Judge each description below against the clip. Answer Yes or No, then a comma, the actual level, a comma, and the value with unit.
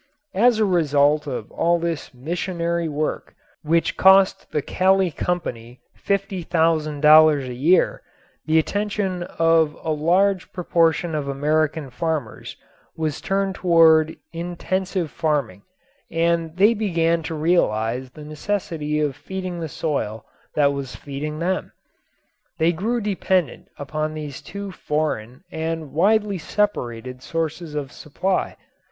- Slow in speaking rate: Yes, slow, 120 wpm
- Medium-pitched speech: Yes, medium, 160 Hz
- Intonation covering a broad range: No, average, 3.4 semitones